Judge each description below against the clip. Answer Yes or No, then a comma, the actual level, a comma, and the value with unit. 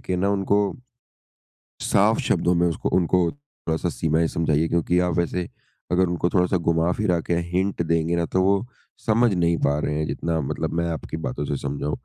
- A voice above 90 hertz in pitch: No, very low, 85 Hz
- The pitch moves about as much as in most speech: No, narrow, 2.1 semitones